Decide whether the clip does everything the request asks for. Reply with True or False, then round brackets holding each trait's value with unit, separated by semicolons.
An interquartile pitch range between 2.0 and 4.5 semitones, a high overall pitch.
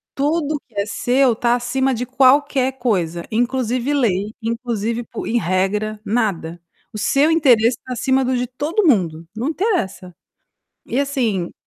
True (4.1 semitones; 240 Hz)